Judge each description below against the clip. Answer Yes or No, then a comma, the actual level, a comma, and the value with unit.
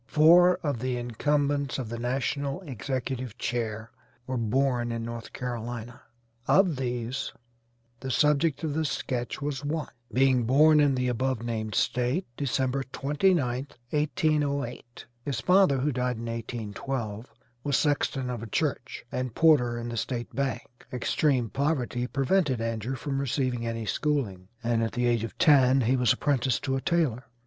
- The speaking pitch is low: Yes, low, 130 Hz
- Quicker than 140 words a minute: Yes, average, 155 wpm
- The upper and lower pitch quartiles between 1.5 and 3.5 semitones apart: Yes, average, 3.2 semitones